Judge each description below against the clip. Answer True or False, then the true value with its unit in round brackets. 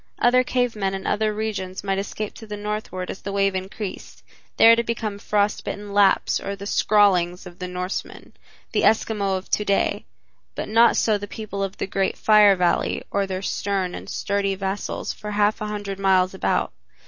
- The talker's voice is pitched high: True (200 Hz)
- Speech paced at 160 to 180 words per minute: False (190 wpm)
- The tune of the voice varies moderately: False (1.7 semitones)